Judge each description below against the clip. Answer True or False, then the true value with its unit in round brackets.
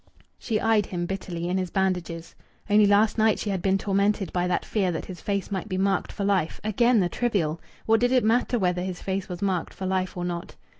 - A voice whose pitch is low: False (190 Hz)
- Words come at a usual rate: False (230 wpm)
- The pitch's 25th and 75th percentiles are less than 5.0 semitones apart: True (2.8 semitones)